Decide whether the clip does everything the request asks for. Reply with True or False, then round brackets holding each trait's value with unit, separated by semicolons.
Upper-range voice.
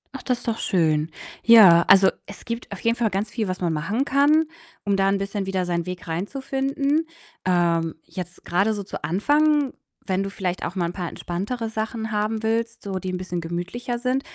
True (200 Hz)